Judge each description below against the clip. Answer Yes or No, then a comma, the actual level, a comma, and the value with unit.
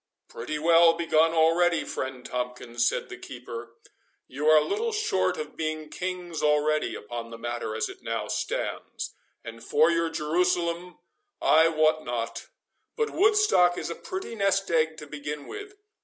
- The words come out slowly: No, average, 155 wpm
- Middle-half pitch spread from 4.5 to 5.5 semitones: Yes, average, 4.9 semitones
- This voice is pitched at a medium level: Yes, medium, 160 Hz